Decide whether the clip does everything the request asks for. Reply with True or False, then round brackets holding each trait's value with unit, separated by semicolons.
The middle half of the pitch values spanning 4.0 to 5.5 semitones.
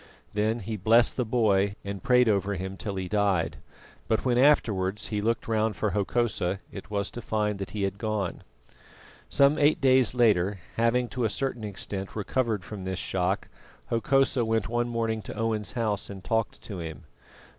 False (3.0 semitones)